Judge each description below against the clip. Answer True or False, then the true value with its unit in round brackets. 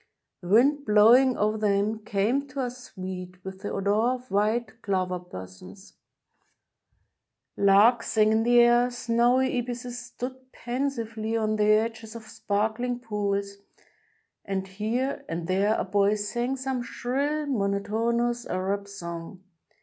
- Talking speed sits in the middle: False (130 wpm)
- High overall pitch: True (220 Hz)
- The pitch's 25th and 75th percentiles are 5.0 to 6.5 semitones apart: False (3.5 semitones)